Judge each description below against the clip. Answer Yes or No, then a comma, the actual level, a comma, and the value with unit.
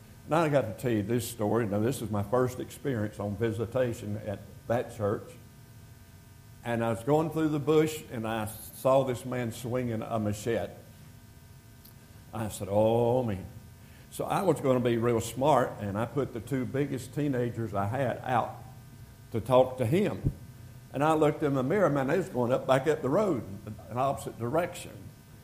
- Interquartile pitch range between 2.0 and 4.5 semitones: Yes, average, 2.8 semitones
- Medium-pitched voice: No, low, 120 Hz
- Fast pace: No, average, 185 wpm